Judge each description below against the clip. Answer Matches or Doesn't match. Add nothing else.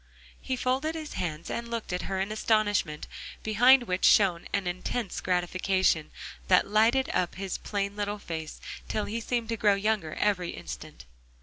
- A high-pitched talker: Matches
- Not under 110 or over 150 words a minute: Doesn't match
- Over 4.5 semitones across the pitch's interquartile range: Doesn't match